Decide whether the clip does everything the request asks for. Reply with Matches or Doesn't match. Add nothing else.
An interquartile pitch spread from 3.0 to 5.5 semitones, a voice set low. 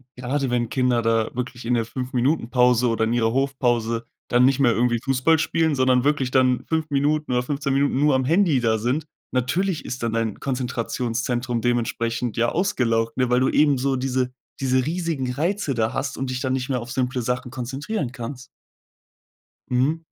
Doesn't match